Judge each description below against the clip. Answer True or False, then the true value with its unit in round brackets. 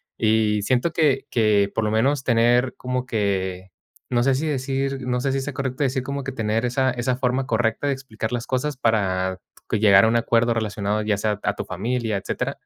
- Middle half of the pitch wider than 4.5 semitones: False (3.6 semitones)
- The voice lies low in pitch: True (120 Hz)